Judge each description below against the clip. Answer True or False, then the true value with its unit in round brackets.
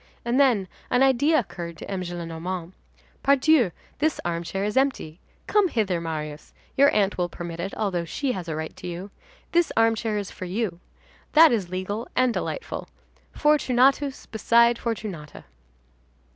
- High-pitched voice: True (205 Hz)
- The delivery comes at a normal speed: True (145 wpm)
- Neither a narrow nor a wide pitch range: False (6.6 semitones)